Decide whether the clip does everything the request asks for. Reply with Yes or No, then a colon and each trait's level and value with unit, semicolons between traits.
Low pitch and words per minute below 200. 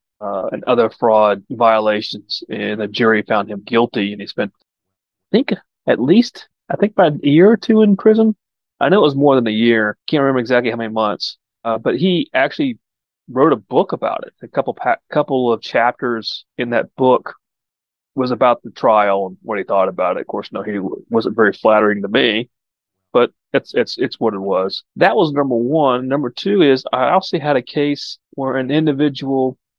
No: low, 125 Hz; fast, 205 wpm